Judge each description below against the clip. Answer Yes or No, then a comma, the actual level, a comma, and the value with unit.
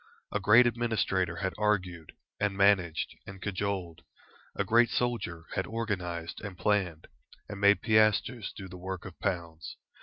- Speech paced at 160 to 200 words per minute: No, average, 145 wpm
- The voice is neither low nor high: No, very low, 95 Hz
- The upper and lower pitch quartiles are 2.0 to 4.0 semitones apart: Yes, average, 3.3 semitones